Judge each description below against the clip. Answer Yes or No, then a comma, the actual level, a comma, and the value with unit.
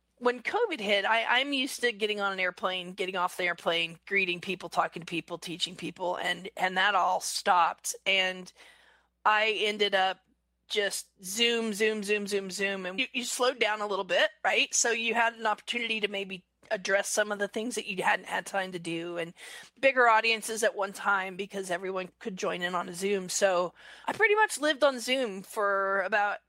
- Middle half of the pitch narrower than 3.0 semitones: No, average, 3.7 semitones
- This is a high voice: Yes, high, 200 Hz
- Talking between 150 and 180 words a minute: No, average, 200 wpm